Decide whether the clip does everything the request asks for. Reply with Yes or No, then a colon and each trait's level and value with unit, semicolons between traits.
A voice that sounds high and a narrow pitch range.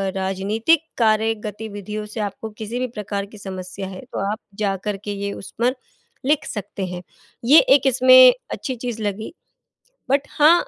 No: high, 215 Hz; average, 4.1 semitones